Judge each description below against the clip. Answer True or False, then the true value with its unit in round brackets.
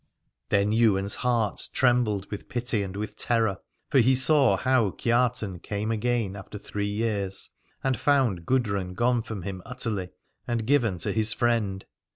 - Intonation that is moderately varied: True (3.5 semitones)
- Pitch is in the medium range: False (110 Hz)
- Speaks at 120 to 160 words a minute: True (155 wpm)